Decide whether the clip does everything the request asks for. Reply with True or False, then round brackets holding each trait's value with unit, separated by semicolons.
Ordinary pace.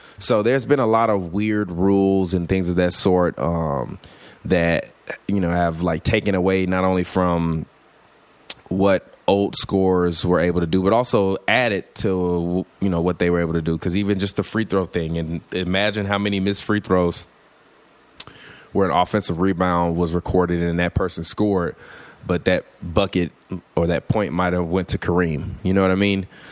True (190 wpm)